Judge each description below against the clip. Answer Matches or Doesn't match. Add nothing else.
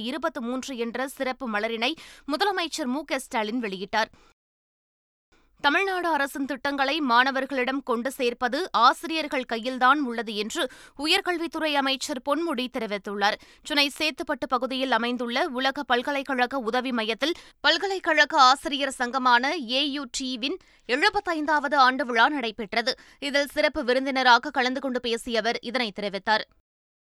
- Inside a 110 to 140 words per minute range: Matches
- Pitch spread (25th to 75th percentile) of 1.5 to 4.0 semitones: Matches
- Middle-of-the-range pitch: Doesn't match